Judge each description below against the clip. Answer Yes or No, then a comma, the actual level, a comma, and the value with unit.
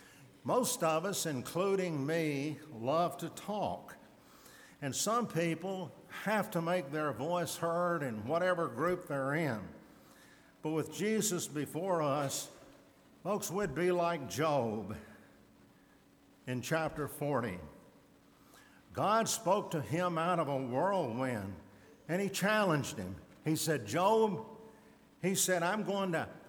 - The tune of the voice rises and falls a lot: No, average, 4.5 semitones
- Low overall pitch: No, medium, 165 Hz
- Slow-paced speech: Yes, slow, 125 wpm